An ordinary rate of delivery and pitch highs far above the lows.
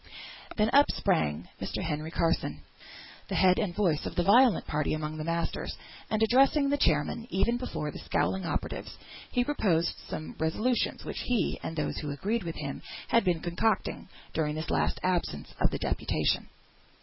Yes: average, 170 wpm; wide, 6.4 semitones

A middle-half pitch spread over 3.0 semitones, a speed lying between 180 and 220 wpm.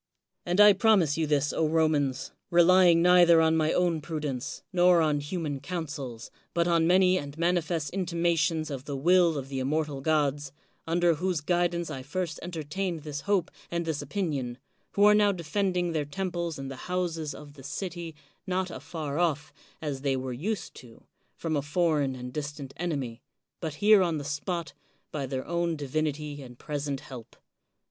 No: average, 3.4 semitones; average, 170 wpm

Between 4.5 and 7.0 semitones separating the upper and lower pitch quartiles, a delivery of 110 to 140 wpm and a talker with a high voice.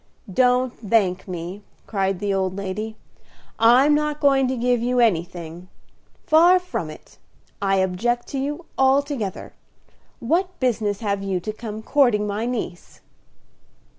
Yes: average, 5.3 semitones; slow, 135 wpm; high, 225 Hz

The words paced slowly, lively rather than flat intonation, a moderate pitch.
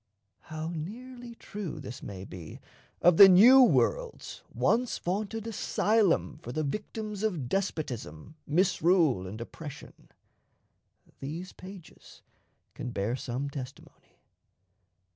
Yes: slow, 105 wpm; wide, 7.7 semitones; medium, 175 Hz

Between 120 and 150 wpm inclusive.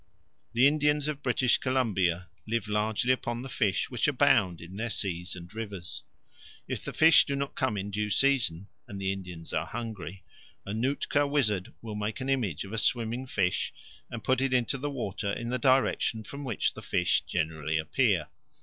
No: average, 185 wpm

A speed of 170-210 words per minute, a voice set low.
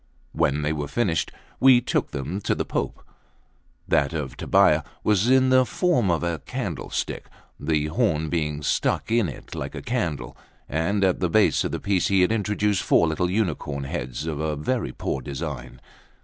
Yes: average, 175 wpm; very low, 85 Hz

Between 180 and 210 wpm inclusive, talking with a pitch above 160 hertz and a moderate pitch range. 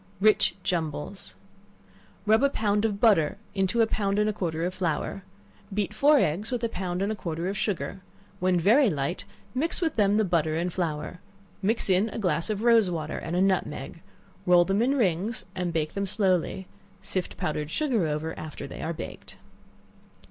Yes: average, 185 wpm; high, 190 Hz; average, 4.3 semitones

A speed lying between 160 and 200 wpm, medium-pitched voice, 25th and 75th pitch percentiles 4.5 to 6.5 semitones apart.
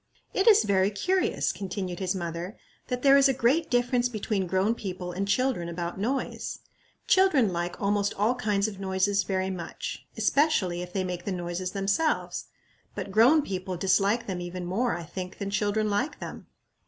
No: average, 175 wpm; high, 200 Hz; average, 4.8 semitones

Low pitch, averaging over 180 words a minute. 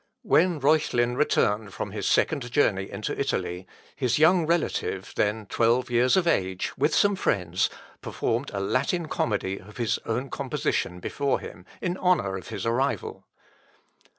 No: low, 120 Hz; average, 150 wpm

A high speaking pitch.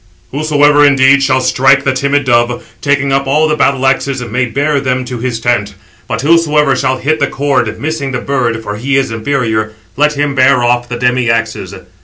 No: low, 135 Hz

